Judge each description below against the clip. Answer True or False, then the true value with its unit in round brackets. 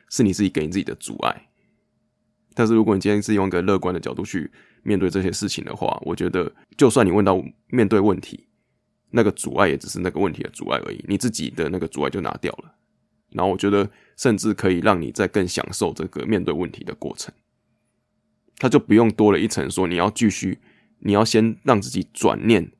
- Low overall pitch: True (100 Hz)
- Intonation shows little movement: True (2.1 semitones)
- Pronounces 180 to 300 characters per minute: False (320 characters per minute)